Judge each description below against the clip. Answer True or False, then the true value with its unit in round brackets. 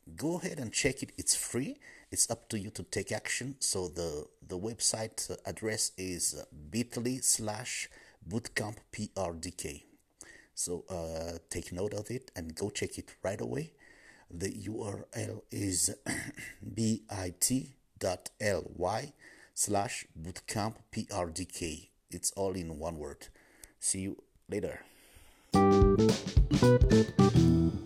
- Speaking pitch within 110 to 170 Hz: False (100 Hz)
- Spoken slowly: True (115 wpm)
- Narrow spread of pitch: False (3.9 semitones)